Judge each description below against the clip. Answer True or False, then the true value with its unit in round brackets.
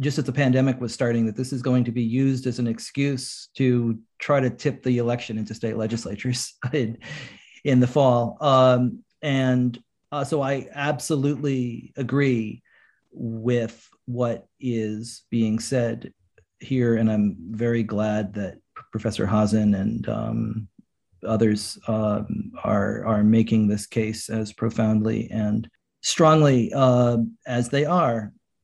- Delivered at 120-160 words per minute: True (140 wpm)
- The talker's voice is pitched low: True (120 Hz)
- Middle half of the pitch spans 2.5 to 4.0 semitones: True (2.9 semitones)